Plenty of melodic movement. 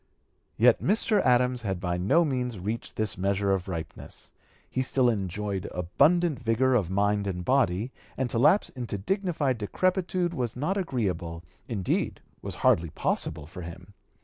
Yes: wide, 5.9 semitones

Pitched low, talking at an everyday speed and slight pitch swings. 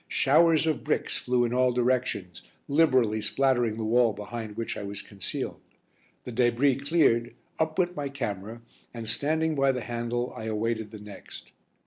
No: low, 120 Hz; average, 160 wpm; average, 3.7 semitones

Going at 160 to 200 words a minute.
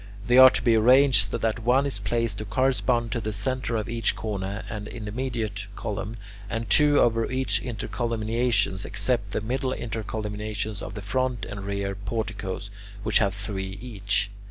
Yes: average, 165 wpm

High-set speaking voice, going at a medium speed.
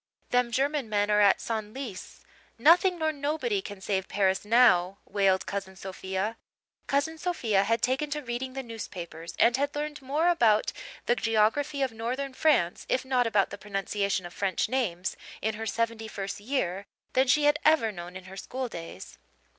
Yes: high, 225 Hz; average, 170 wpm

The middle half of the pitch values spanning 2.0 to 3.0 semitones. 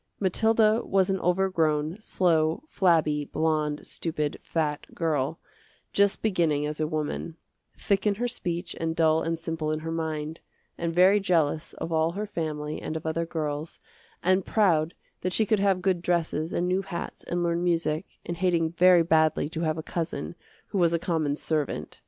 Yes: average, 2.7 semitones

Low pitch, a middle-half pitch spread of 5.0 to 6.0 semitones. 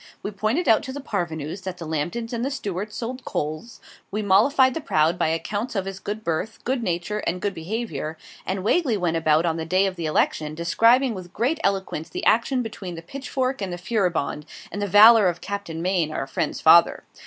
No: high, 195 Hz; wide, 5.4 semitones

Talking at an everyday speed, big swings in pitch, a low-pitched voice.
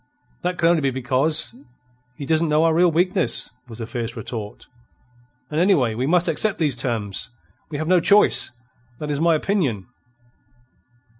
No: average, 160 wpm; wide, 5.8 semitones; medium, 155 Hz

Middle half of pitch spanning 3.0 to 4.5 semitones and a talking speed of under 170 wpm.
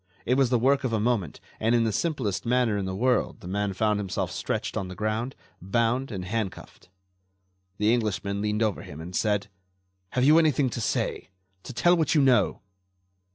No: average, 3.9 semitones; average, 195 wpm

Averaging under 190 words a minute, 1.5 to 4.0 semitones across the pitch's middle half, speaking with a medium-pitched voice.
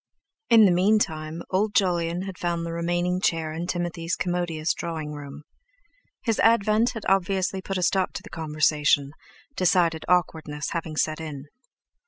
Yes: average, 150 wpm; average, 3.0 semitones; medium, 170 Hz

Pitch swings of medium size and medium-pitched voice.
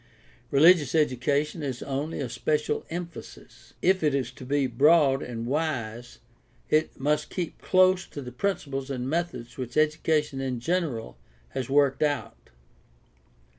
Yes: average, 3.6 semitones; medium, 145 Hz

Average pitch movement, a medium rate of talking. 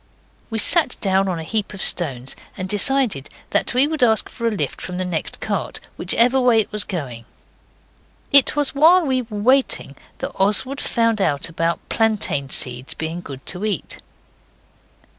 No: wide, 6.9 semitones; average, 170 wpm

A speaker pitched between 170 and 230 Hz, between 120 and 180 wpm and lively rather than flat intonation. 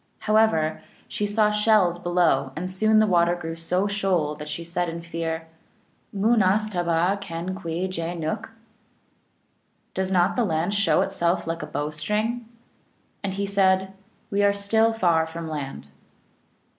No: medium, 185 Hz; average, 170 wpm; average, 3.6 semitones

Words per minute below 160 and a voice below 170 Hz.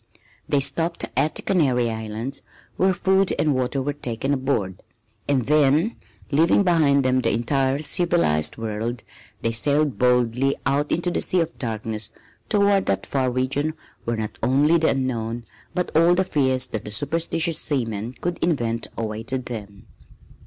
Yes: average, 150 wpm; low, 135 Hz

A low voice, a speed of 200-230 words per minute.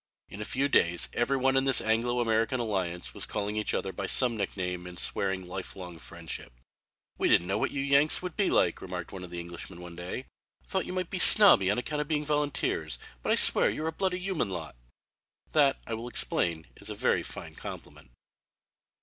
Yes: low, 110 Hz; fast, 205 wpm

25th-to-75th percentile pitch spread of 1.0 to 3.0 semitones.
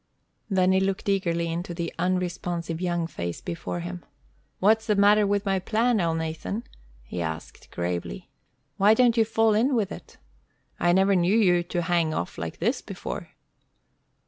No: average, 3.8 semitones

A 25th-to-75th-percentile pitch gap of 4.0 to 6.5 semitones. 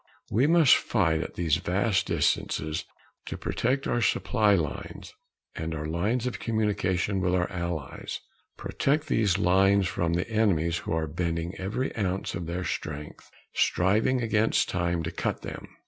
Yes: average, 4.5 semitones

